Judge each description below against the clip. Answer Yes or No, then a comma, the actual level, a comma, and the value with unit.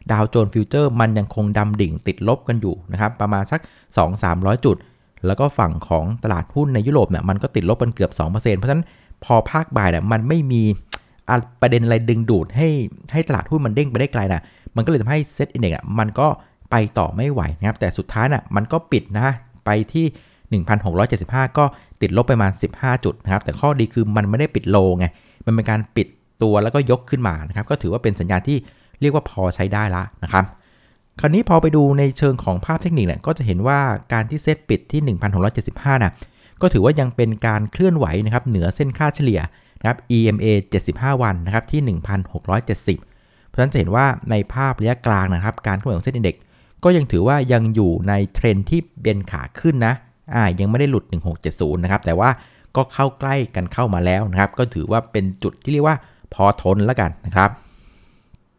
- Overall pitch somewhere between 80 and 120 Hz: Yes, low, 110 Hz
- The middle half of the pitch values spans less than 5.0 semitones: No, wide, 5.6 semitones